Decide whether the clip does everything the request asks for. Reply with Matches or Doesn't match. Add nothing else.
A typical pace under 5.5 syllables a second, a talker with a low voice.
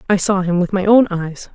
Doesn't match